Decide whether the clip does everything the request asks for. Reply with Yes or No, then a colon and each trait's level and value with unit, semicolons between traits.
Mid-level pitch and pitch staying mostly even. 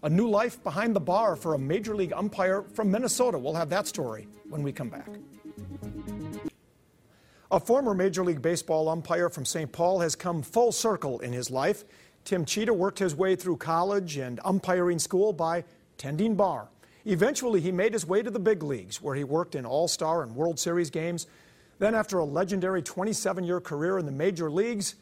No: medium, 175 Hz; average, 4.6 semitones